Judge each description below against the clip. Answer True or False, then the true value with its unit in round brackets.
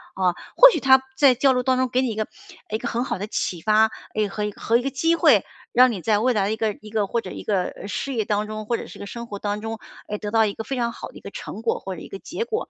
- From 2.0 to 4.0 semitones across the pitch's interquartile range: True (3.4 semitones)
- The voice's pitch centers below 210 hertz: False (220 Hz)